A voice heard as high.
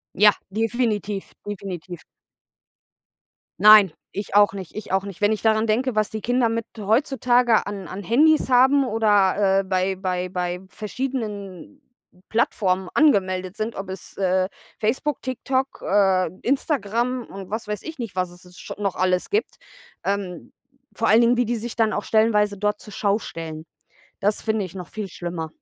Yes: high, 210 Hz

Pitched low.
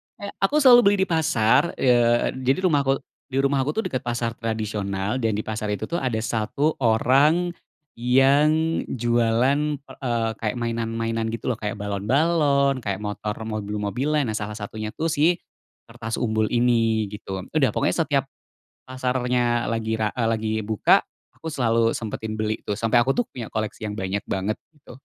Yes: low, 115 Hz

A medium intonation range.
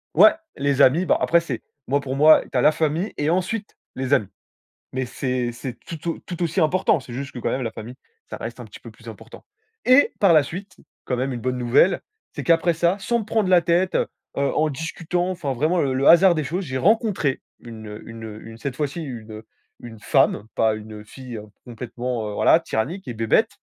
No: wide, 5.9 semitones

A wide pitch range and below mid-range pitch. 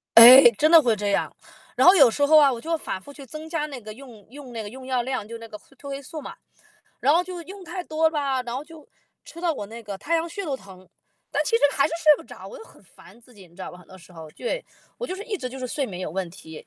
No: wide, 6.5 semitones; very high, 265 Hz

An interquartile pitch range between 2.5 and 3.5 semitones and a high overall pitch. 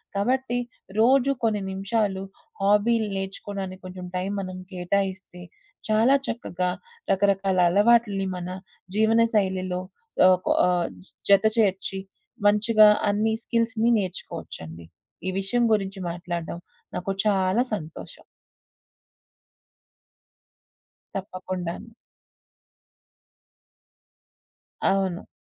Yes: average, 2.8 semitones; high, 195 Hz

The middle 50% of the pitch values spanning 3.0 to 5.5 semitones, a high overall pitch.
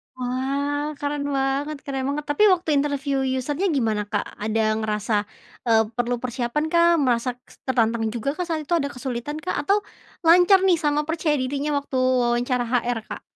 Yes: average, 3.7 semitones; very high, 270 Hz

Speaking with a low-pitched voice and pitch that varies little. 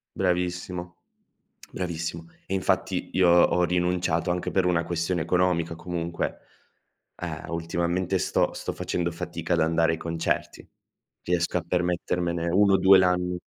Yes: very low, 85 Hz; narrow, 1.2 semitones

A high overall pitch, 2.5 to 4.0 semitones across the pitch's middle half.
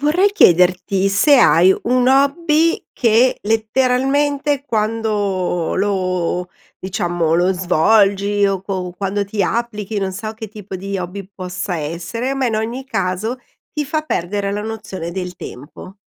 No: high, 205 Hz; average, 4.9 semitones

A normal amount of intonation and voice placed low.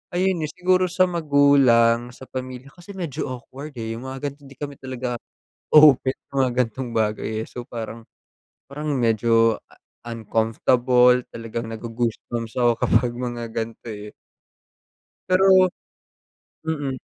Yes: average, 3.6 semitones; low, 125 Hz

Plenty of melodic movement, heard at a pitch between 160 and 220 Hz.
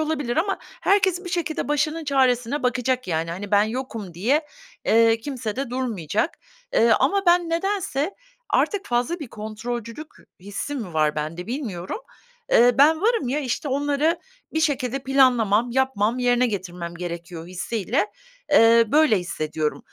No: wide, 6.3 semitones; high, 245 Hz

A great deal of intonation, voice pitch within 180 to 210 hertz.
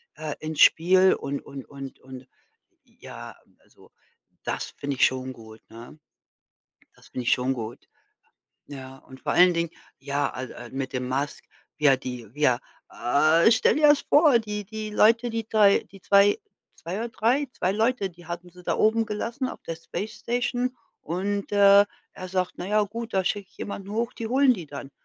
Yes: wide, 7.7 semitones; medium, 185 Hz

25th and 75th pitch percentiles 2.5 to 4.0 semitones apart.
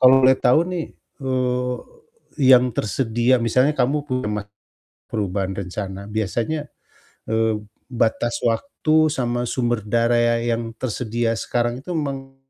Yes: average, 2.8 semitones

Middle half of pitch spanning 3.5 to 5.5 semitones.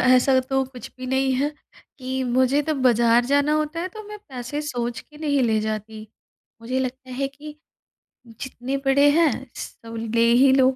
No: average, 2.8 semitones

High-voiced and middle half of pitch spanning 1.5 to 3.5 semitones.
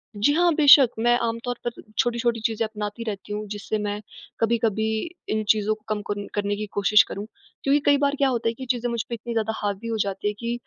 Yes: high, 225 Hz; narrow, 2.5 semitones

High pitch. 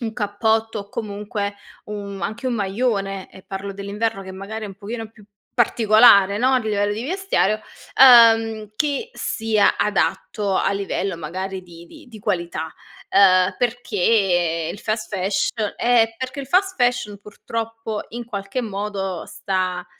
Yes: high, 210 Hz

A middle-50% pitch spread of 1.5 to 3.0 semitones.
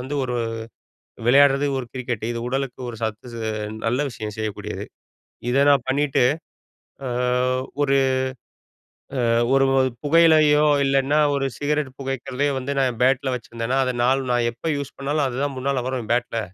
Yes: narrow, 2.4 semitones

